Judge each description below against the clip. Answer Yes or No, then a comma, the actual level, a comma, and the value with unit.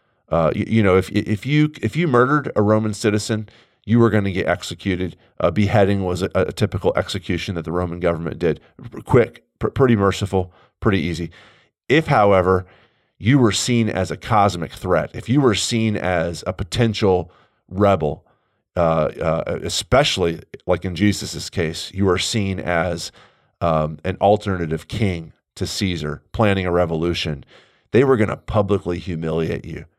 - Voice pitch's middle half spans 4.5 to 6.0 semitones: No, average, 3.7 semitones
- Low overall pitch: Yes, very low, 95 Hz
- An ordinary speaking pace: Yes, average, 160 wpm